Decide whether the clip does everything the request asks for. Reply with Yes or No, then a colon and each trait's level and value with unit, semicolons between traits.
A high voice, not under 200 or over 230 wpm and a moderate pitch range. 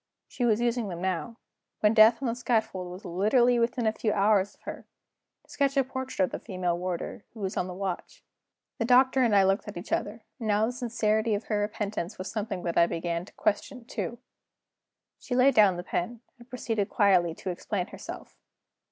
Yes: high, 215 Hz; fast, 205 wpm; average, 4.1 semitones